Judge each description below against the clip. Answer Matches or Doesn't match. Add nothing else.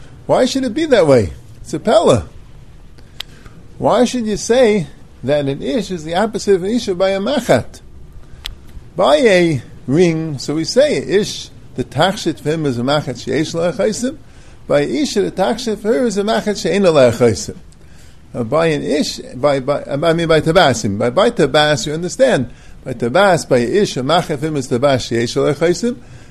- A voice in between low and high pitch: Matches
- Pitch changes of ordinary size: Doesn't match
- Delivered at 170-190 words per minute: Matches